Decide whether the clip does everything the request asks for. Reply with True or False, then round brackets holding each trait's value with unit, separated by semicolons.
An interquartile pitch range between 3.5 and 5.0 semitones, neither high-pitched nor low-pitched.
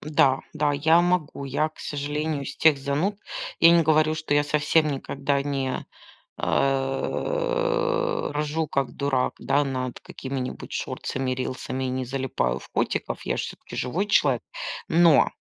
False (3.1 semitones; 145 Hz)